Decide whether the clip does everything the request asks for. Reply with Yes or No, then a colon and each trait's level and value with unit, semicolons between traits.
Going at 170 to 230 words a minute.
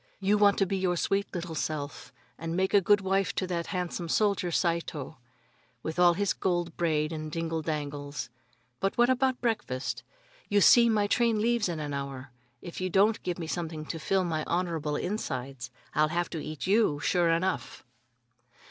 Yes: average, 180 wpm